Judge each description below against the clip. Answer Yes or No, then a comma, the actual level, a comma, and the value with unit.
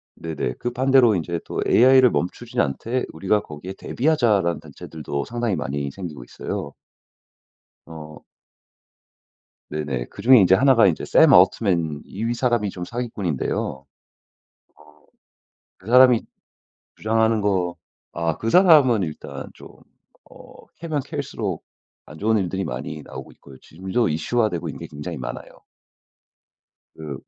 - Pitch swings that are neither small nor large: No, wide, 7.2 semitones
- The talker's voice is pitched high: No, very low, 95 Hz